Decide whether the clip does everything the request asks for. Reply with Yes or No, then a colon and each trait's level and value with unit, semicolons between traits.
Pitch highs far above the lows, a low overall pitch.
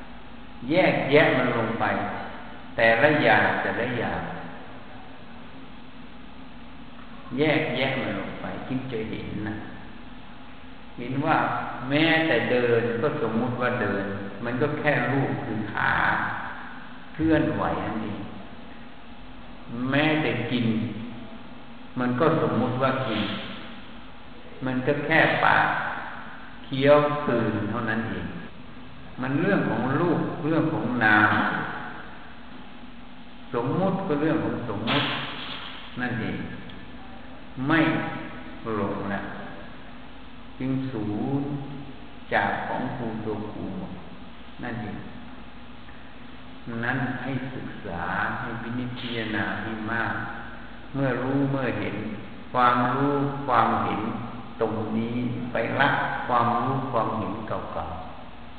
No: average, 4.4 semitones; low, 120 Hz